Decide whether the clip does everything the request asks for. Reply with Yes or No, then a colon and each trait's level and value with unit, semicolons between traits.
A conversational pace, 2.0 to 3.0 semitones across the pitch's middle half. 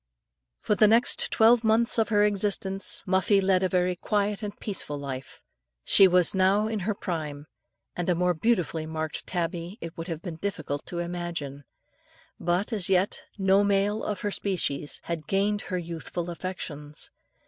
No: average, 165 wpm; average, 3.5 semitones